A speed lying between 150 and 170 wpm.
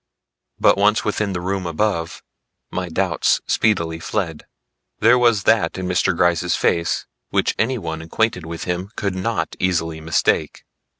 No: average, 140 wpm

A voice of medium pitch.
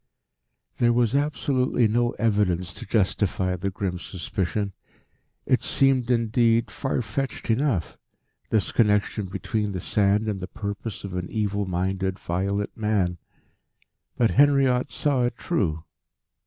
No: low, 105 Hz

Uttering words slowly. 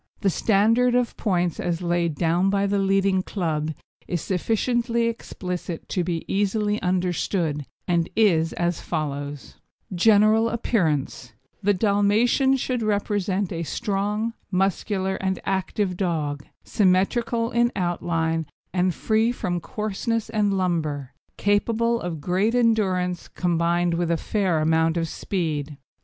Yes: slow, 125 wpm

